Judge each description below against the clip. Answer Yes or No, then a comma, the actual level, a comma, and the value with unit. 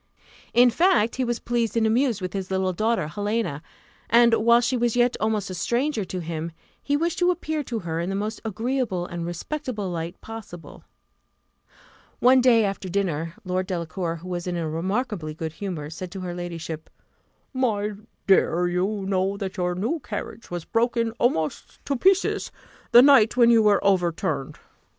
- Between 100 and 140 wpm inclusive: No, average, 175 wpm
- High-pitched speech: Yes, high, 200 Hz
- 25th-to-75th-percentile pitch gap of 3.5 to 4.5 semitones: No, average, 5.2 semitones